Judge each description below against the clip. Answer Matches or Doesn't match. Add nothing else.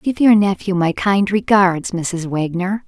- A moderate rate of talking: Matches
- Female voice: Matches